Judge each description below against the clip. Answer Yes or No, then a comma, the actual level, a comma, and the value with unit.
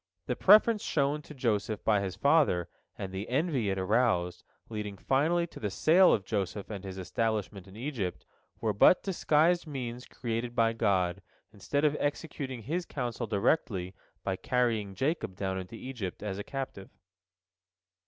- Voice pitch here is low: Yes, low, 115 Hz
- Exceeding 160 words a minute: No, average, 155 wpm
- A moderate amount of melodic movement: No, wide, 6.1 semitones